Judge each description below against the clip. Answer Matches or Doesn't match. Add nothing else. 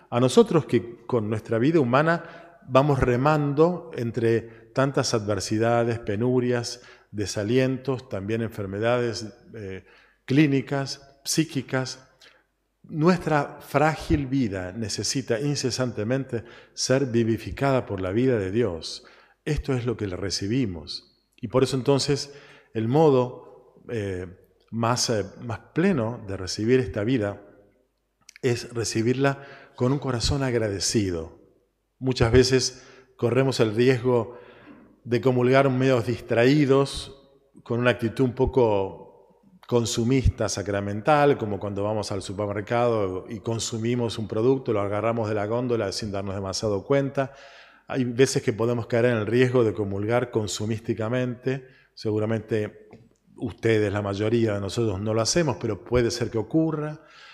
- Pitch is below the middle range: Matches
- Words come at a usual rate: Doesn't match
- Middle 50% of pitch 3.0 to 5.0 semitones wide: Matches